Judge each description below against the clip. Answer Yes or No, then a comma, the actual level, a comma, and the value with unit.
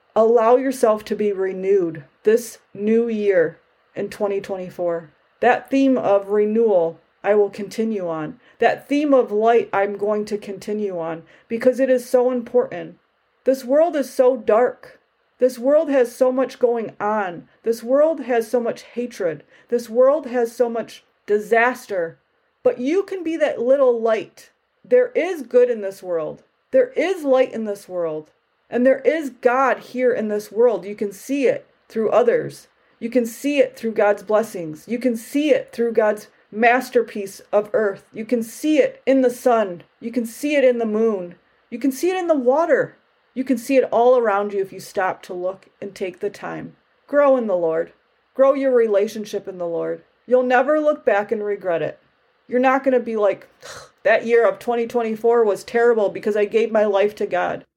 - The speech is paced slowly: No, average, 185 wpm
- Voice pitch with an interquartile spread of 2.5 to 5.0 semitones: Yes, average, 4.0 semitones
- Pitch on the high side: Yes, high, 235 Hz